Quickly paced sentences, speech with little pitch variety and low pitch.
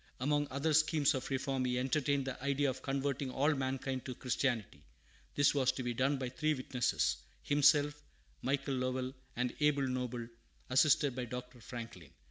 No: average, 160 wpm; narrow, 2.0 semitones; low, 130 Hz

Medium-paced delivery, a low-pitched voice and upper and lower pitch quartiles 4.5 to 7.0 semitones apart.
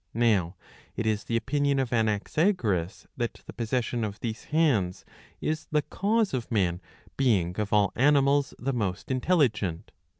Yes: average, 145 wpm; low, 115 Hz; wide, 5.5 semitones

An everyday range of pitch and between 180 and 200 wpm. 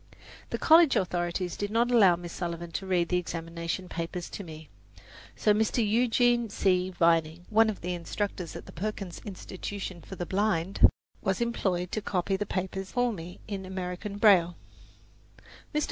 No: average, 3.2 semitones; average, 160 wpm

